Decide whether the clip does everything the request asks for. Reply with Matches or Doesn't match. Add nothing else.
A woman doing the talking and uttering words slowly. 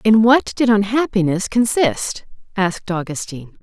Matches